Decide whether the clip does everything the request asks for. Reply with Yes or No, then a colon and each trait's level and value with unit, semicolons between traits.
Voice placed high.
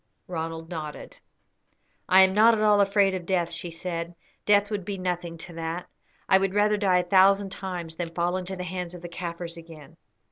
No: medium, 180 Hz